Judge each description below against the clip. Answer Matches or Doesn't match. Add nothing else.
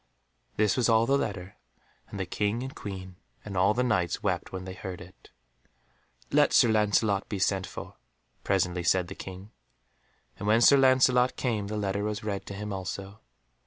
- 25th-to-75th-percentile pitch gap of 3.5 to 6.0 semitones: Doesn't match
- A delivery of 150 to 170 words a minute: Doesn't match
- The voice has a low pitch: Matches